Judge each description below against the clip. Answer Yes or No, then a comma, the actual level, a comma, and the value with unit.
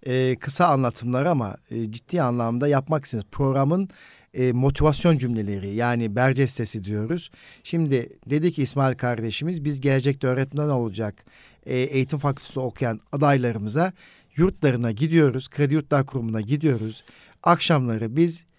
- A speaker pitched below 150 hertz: Yes, low, 135 Hz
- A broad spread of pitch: No, average, 3.9 semitones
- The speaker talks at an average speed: Yes, average, 125 wpm